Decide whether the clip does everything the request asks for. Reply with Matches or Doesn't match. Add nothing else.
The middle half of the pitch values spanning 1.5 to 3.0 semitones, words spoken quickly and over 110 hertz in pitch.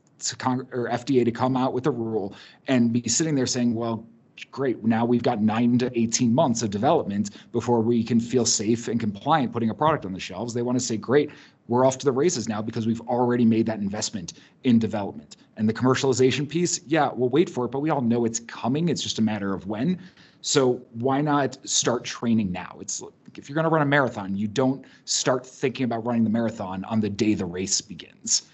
Matches